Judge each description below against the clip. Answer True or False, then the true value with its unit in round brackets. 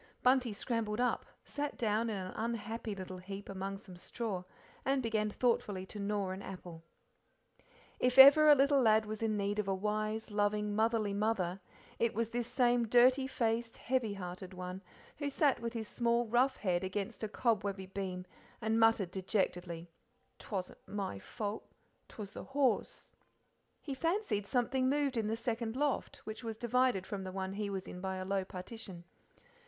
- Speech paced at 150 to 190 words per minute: True (170 wpm)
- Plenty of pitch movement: False (3.7 semitones)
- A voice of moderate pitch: False (215 Hz)